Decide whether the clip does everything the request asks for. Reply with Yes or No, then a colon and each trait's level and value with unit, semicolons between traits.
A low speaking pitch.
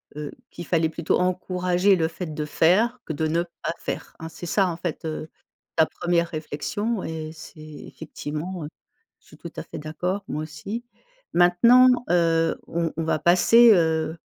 No: medium, 170 Hz